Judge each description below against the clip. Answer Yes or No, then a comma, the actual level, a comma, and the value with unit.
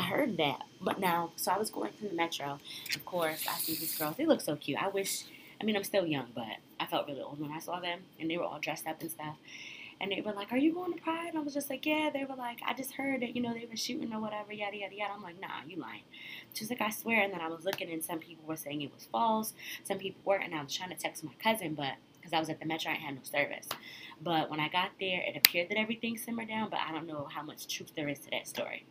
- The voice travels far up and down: Yes, wide, 5.7 semitones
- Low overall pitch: No, medium, 180 Hz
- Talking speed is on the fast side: Yes, fast, 300 wpm